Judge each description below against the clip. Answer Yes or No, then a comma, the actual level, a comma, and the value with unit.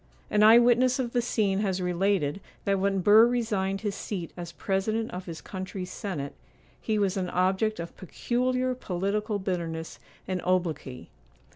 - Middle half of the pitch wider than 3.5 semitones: No, average, 3.2 semitones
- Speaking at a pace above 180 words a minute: No, average, 155 wpm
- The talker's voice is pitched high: Yes, high, 195 Hz